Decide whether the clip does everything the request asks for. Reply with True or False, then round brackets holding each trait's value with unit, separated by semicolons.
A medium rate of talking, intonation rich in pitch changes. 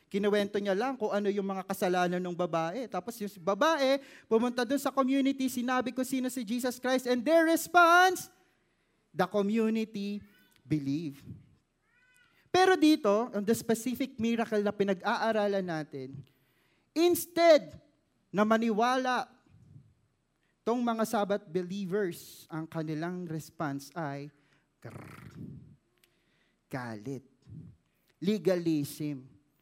False (105 wpm; 7.3 semitones)